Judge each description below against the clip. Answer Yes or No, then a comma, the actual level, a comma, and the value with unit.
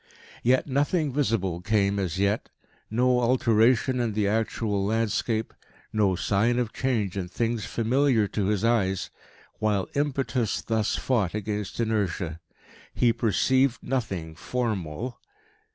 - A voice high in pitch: No, low, 110 Hz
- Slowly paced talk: Yes, slow, 125 wpm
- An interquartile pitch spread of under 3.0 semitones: No, average, 3.7 semitones